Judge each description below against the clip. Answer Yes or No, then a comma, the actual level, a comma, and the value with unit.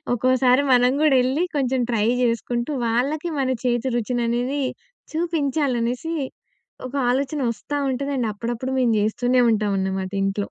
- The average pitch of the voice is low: No, very high, 250 Hz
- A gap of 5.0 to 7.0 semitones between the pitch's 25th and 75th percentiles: No, average, 2.9 semitones